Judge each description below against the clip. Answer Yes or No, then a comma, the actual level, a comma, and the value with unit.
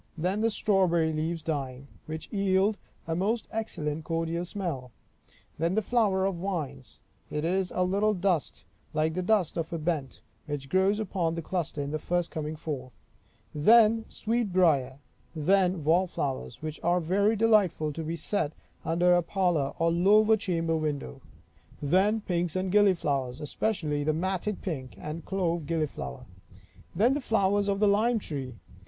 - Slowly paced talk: No, average, 160 wpm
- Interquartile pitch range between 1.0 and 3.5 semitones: No, average, 4.3 semitones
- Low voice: No, medium, 170 Hz